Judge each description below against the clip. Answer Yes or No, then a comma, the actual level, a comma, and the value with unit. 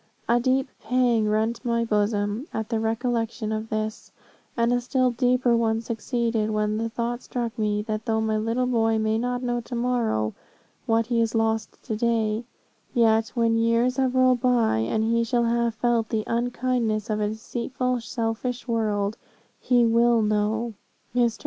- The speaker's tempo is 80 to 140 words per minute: No, average, 170 wpm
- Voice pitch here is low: No, high, 230 Hz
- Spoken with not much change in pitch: Yes, narrow, 1.7 semitones